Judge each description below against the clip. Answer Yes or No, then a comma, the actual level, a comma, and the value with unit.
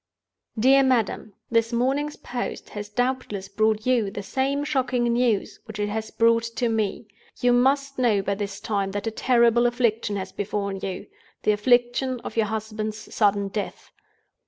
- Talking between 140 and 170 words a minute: Yes, average, 160 wpm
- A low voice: No, high, 225 Hz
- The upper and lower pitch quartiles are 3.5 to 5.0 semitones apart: No, average, 3.1 semitones